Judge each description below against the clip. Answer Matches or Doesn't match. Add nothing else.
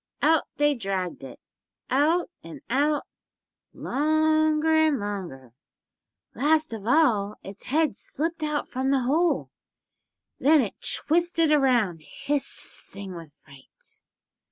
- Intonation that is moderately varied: Doesn't match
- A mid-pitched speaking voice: Doesn't match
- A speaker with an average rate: Doesn't match